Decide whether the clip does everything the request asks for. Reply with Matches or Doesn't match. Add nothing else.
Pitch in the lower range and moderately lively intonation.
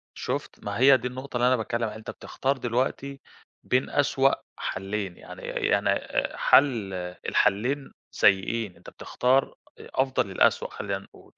Matches